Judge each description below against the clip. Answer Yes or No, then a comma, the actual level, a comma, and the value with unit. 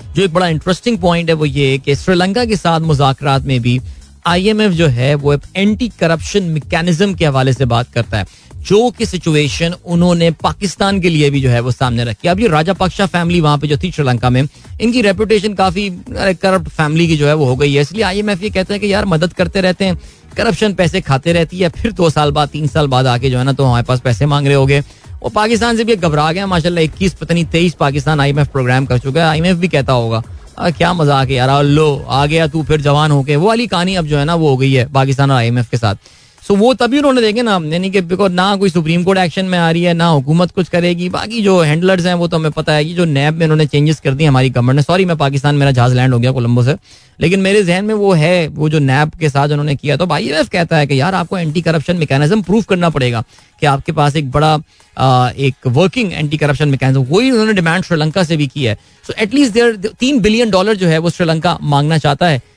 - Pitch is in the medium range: Yes, medium, 160 Hz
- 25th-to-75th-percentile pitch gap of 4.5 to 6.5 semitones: Yes, average, 4.9 semitones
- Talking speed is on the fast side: Yes, fast, 245 wpm